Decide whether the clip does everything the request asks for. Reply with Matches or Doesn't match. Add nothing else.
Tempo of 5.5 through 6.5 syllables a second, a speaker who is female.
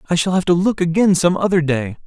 Doesn't match